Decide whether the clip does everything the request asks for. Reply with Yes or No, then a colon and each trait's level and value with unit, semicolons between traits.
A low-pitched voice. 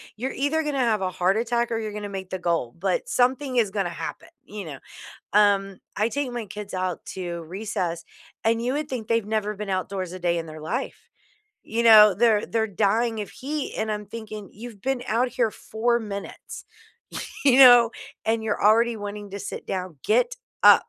No: high, 215 Hz